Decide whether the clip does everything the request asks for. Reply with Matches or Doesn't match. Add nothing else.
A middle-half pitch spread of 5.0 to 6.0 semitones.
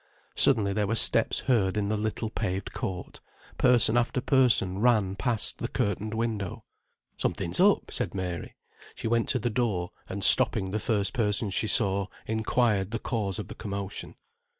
Doesn't match